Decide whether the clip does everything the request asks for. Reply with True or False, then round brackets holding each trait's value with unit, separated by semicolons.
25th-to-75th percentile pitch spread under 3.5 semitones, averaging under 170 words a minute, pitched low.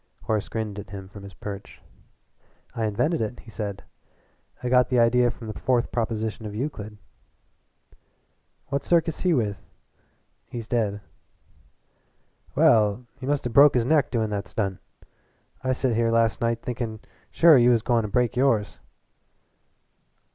True (2.9 semitones; 150 wpm; 115 Hz)